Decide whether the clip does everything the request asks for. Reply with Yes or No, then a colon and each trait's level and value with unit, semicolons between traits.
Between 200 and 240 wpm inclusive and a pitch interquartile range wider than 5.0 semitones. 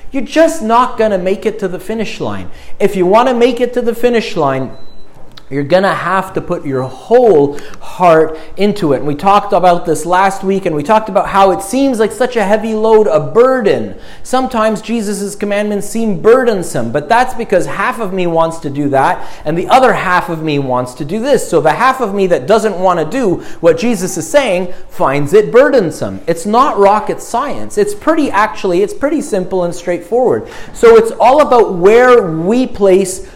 Yes: fast, 205 wpm; wide, 5.5 semitones